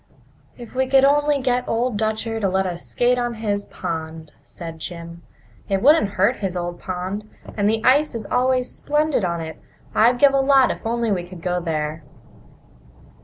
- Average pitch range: No, wide, 6.0 semitones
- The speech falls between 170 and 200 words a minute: Yes, average, 180 wpm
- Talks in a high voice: Yes, high, 215 Hz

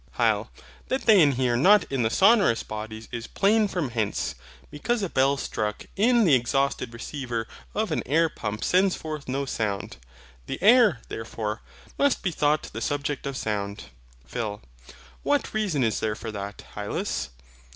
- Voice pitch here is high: No, low, 135 Hz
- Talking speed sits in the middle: Yes, average, 160 wpm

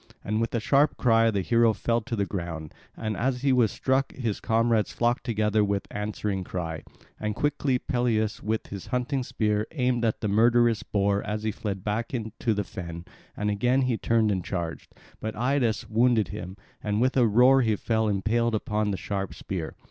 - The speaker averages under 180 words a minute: No, average, 190 wpm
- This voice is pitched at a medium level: No, low, 110 Hz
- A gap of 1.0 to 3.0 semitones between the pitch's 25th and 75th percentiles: Yes, average, 2.7 semitones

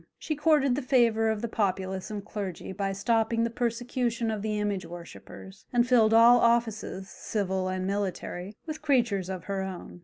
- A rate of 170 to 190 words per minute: Yes, average, 175 wpm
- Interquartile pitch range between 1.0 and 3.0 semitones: No, average, 3.7 semitones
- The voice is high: Yes, high, 215 Hz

